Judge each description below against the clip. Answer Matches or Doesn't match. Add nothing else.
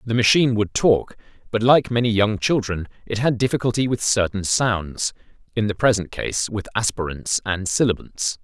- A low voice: Matches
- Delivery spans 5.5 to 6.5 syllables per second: Doesn't match